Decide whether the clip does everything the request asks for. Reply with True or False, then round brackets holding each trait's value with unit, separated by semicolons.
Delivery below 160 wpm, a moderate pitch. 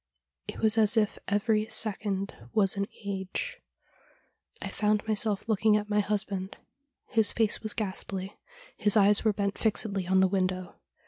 False (150 wpm; 205 Hz)